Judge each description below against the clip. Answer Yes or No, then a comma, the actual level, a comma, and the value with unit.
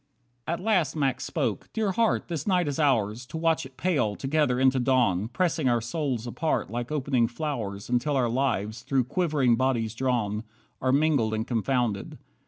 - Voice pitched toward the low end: Yes, low, 130 Hz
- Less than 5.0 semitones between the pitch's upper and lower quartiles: Yes, average, 4.6 semitones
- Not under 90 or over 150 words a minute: No, average, 175 wpm